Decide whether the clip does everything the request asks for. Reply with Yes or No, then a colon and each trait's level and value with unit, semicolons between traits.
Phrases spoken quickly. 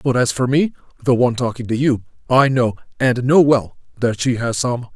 No: average, 195 wpm